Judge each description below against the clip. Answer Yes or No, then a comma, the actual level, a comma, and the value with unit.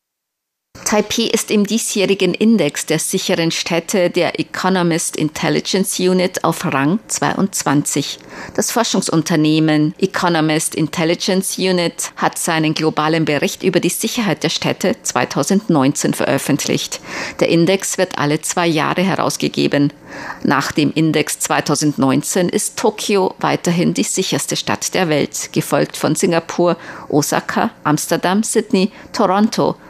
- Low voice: No, medium, 175 Hz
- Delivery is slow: Yes, slow, 115 wpm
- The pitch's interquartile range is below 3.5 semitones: No, average, 3.9 semitones